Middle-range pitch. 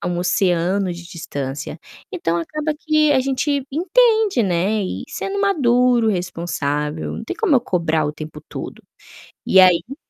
No: high, 195 Hz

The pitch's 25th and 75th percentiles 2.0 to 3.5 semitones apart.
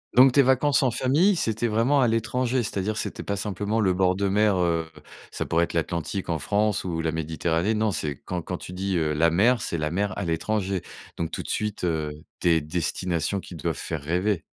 No: average, 4.6 semitones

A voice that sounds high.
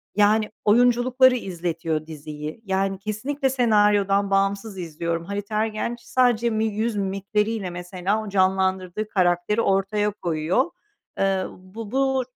Yes: high, 200 Hz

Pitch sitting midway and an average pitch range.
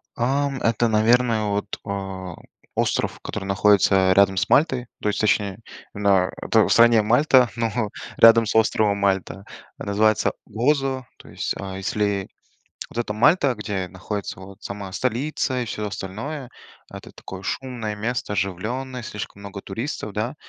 No: low, 105 Hz; average, 3.6 semitones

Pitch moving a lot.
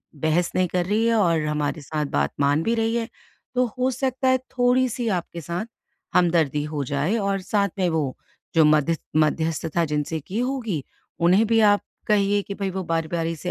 Yes: wide, 6.2 semitones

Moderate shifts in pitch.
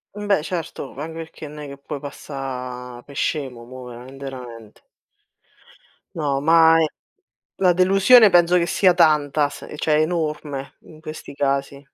Yes: average, 3.3 semitones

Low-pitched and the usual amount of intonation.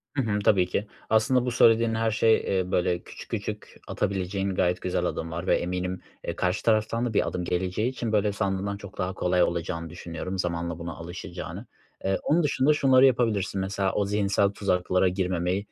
Yes: very low, 95 Hz; average, 3.5 semitones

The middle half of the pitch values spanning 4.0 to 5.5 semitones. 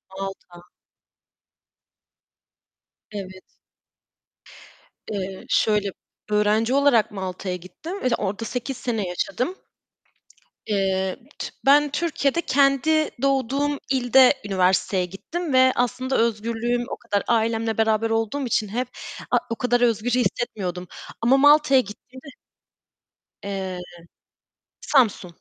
Yes: average, 4.9 semitones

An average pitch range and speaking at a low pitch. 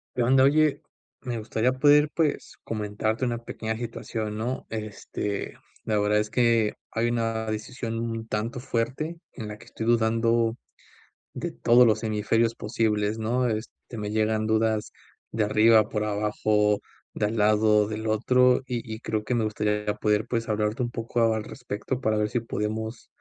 No: narrow, 1.7 semitones; low, 110 Hz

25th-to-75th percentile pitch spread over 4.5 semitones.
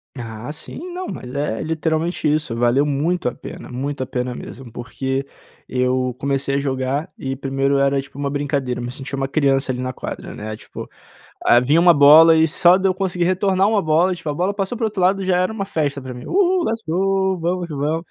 Yes: average, 5.3 semitones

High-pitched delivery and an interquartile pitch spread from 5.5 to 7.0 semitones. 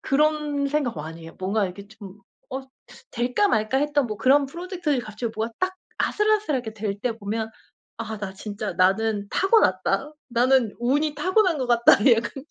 Yes: high, 240 Hz; wide, 5.8 semitones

